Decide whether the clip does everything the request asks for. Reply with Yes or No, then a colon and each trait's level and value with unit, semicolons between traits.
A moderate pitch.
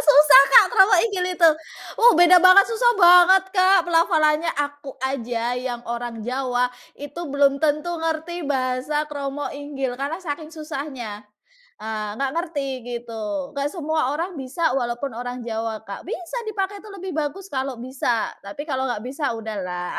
No: very high, 285 Hz